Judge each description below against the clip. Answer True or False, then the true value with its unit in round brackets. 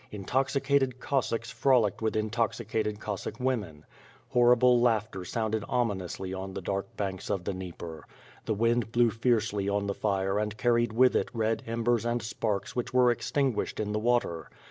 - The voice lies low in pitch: True (110 Hz)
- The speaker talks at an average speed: True (165 wpm)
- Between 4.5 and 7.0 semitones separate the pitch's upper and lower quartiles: False (3.3 semitones)